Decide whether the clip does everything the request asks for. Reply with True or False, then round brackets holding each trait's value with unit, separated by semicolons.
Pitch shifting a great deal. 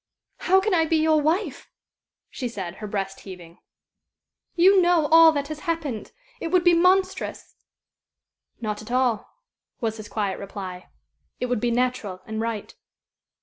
True (7.8 semitones)